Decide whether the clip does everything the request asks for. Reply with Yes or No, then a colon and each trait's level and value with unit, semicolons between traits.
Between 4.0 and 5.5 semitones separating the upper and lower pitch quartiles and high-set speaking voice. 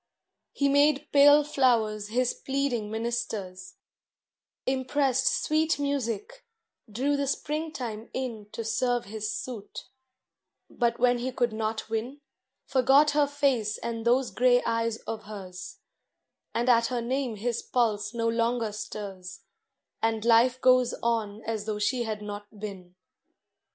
No: average, 3.2 semitones; high, 235 Hz